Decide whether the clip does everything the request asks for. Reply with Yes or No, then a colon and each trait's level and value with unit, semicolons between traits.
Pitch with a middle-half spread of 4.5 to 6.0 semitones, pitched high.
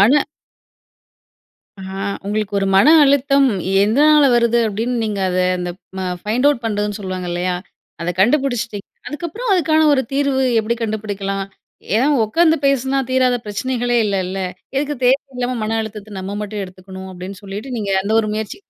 Yes: average, 5.2 semitones; high, 220 Hz